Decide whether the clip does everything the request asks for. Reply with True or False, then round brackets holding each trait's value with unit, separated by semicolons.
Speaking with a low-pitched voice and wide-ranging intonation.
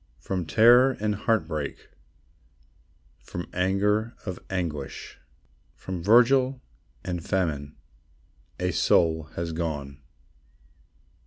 False (90 Hz; 5.0 semitones)